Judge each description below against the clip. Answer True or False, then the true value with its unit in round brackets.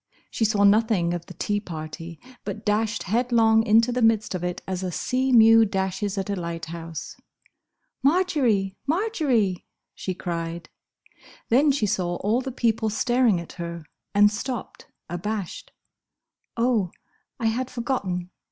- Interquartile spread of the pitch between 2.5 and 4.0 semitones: False (4.8 semitones)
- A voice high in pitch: True (210 Hz)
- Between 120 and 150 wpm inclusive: True (140 wpm)